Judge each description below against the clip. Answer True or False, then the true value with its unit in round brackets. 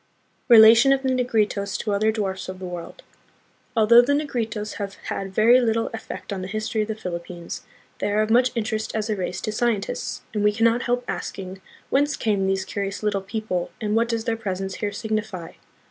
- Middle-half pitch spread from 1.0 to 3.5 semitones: True (2.7 semitones)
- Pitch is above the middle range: True (215 Hz)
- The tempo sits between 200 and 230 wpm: True (205 wpm)